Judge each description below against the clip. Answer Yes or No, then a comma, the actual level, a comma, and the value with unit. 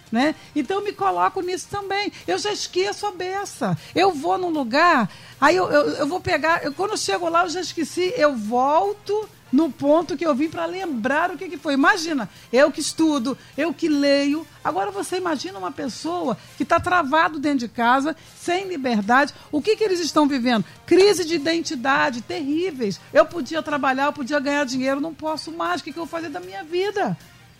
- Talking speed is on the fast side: Yes, fast, 200 wpm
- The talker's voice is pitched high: Yes, very high, 320 Hz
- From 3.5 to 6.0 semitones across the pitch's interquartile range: Yes, average, 3.9 semitones